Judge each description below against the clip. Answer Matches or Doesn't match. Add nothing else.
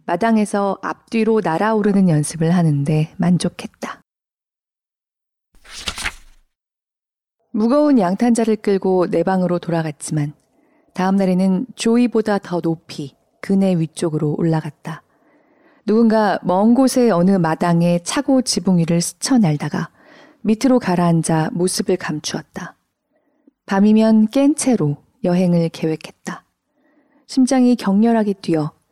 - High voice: Matches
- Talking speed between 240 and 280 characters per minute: Matches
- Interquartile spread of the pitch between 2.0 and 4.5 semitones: Doesn't match